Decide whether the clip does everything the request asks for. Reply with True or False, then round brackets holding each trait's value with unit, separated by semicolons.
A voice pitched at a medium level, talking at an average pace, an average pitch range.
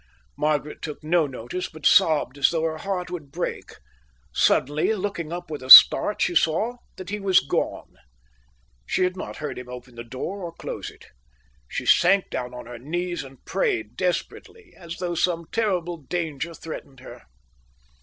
True (165 Hz; 170 wpm; 4.1 semitones)